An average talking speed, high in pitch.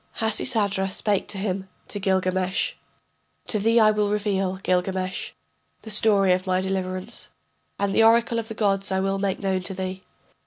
Yes: average, 170 wpm; high, 195 Hz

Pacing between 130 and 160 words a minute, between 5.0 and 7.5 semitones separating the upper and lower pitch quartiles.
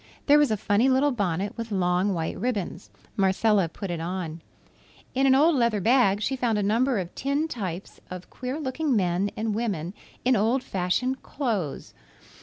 No: average, 175 wpm; wide, 5.6 semitones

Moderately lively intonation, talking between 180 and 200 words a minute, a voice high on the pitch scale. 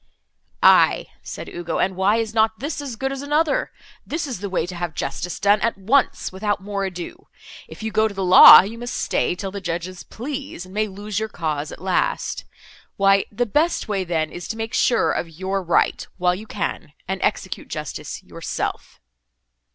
Yes: average, 3.9 semitones; average, 190 wpm; high, 200 Hz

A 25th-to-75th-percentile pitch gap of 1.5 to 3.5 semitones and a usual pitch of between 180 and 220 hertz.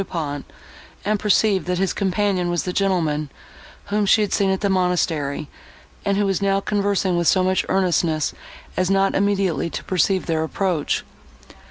Yes: narrow, 2.4 semitones; high, 190 Hz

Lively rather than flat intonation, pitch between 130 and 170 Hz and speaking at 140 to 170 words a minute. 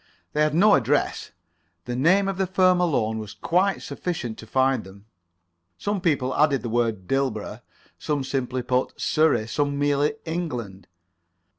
Yes: wide, 6.0 semitones; medium, 140 Hz; average, 150 wpm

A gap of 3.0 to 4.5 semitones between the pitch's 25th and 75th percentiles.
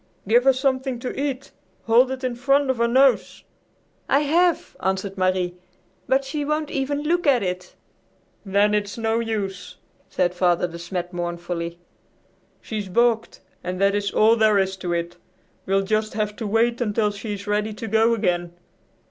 No: average, 5.2 semitones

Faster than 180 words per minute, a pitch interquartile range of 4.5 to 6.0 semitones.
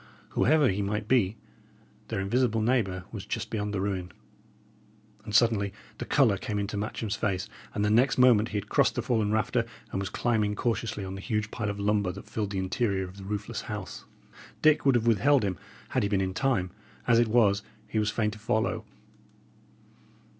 No: average, 190 wpm; average, 2.7 semitones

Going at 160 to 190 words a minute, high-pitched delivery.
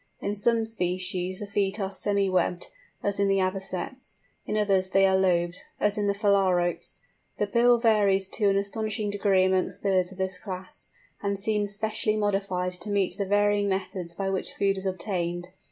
Yes: average, 180 wpm; high, 195 Hz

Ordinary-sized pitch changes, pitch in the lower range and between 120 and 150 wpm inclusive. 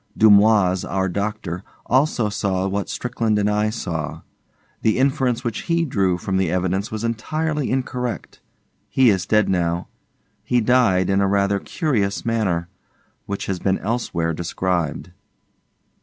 Yes: average, 3.8 semitones; low, 100 Hz; average, 140 wpm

